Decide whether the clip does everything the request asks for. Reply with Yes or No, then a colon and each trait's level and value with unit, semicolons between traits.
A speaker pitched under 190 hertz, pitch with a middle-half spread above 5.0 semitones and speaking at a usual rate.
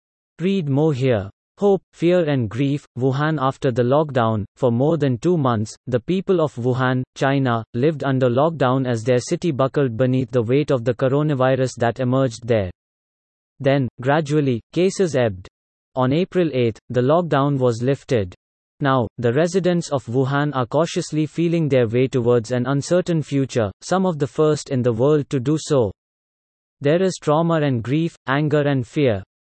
No: low, 135 Hz; average, 3.8 semitones; average, 165 wpm